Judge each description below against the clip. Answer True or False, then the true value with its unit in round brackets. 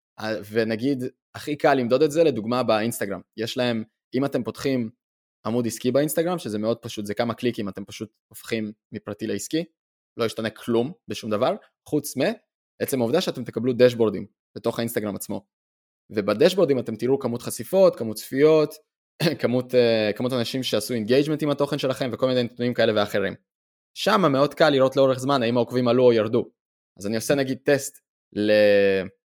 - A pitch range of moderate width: True (3.6 semitones)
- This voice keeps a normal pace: False (160 wpm)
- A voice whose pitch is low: True (120 Hz)